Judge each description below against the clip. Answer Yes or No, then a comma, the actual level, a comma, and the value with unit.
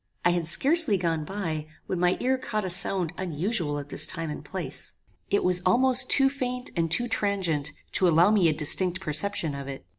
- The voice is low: No, medium, 180 Hz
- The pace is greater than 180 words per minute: Yes, average, 200 wpm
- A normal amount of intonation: Yes, average, 4.9 semitones